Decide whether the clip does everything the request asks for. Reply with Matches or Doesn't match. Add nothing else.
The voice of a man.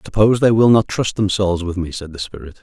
Matches